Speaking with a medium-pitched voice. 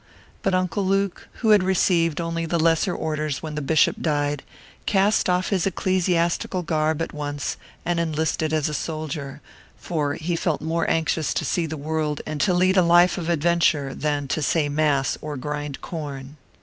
Yes: medium, 160 Hz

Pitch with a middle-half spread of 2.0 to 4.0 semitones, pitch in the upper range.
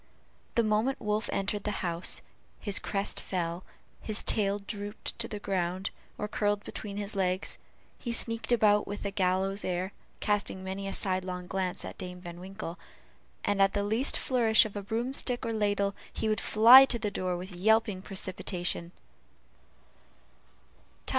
Yes: narrow, 2.4 semitones; high, 200 Hz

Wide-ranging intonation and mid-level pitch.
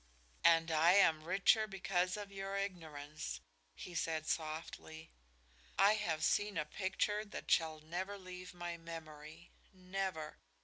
No: average, 3.5 semitones; medium, 175 Hz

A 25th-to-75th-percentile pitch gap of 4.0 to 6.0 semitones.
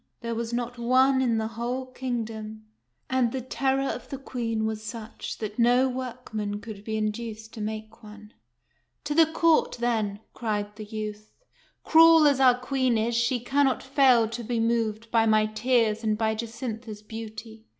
No: average, 2.7 semitones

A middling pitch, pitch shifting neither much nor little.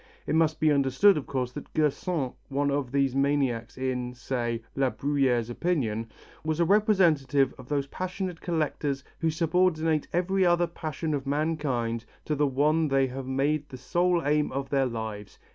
Yes: medium, 145 Hz; average, 3.6 semitones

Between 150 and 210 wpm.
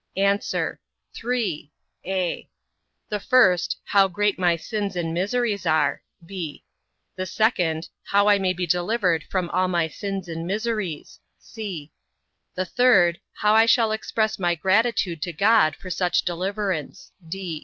No: slow, 135 wpm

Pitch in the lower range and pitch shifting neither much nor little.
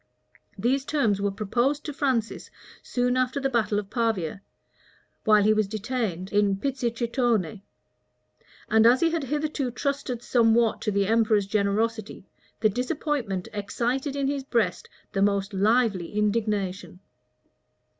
No: high, 225 Hz; average, 3.9 semitones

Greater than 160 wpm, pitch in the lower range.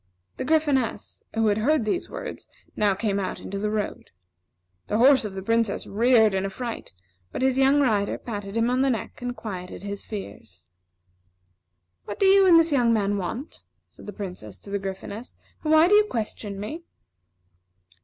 No: average, 180 wpm; high, 220 Hz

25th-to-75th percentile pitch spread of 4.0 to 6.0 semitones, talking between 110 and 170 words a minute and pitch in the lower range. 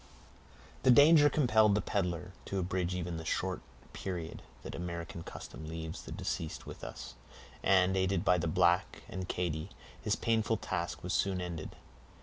No: narrow, 2.5 semitones; average, 155 wpm; very low, 90 Hz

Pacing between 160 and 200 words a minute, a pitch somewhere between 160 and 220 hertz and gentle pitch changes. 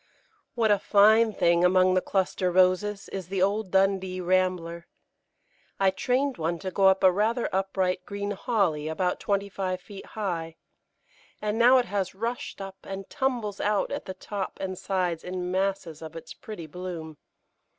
Yes: average, 165 wpm; high, 190 Hz; narrow, 2.1 semitones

